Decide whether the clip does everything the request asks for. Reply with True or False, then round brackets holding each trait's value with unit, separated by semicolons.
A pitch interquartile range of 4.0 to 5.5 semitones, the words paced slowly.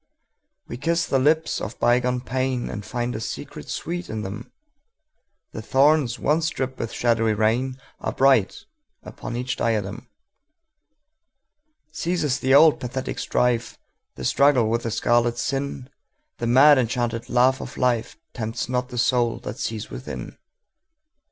True (4.3 semitones; 120 wpm)